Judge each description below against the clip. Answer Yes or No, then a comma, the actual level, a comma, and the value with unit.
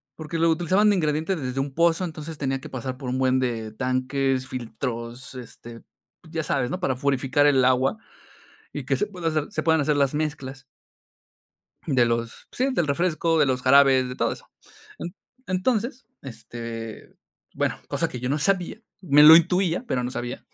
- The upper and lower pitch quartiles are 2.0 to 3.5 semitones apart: No, average, 4.2 semitones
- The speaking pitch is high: No, medium, 140 Hz